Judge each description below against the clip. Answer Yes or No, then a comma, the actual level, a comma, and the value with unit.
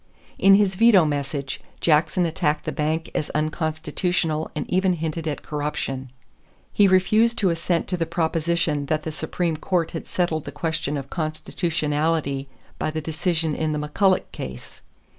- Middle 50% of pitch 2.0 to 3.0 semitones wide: Yes, narrow, 2.6 semitones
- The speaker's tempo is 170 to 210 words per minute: No, average, 155 wpm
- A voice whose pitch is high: No, medium, 160 Hz